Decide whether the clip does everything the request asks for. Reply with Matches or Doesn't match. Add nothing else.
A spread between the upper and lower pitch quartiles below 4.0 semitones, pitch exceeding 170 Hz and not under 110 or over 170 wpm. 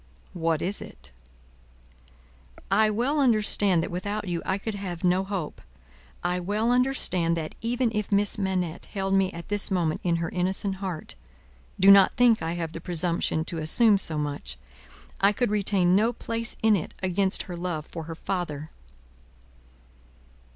Matches